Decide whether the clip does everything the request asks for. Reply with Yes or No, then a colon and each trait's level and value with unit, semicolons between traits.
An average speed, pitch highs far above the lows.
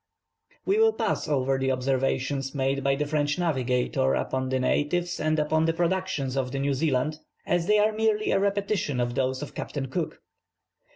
No: average, 170 wpm; average, 4.7 semitones